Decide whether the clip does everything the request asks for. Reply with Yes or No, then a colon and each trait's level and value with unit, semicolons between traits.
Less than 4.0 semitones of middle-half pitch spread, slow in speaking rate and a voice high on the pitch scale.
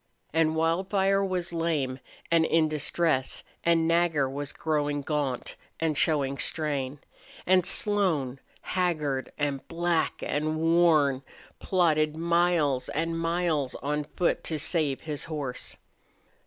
No: average, 2.8 semitones; slow, 115 wpm; medium, 155 Hz